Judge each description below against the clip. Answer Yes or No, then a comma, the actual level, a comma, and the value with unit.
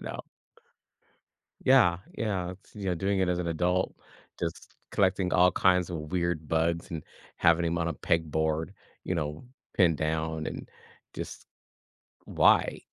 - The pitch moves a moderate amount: No, narrow, 2.3 semitones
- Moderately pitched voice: No, very low, 85 Hz